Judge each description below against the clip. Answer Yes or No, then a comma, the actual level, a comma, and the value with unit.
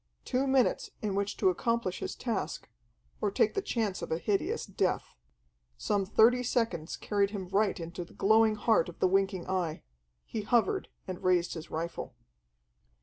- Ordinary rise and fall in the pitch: Yes, average, 3.5 semitones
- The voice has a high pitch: Yes, high, 200 Hz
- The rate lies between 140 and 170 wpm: Yes, average, 165 wpm